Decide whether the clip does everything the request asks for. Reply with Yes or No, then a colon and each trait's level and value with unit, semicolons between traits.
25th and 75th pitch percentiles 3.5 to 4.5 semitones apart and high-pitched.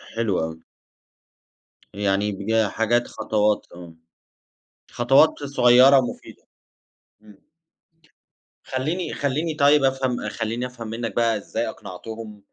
No: average, 4.0 semitones; low, 115 Hz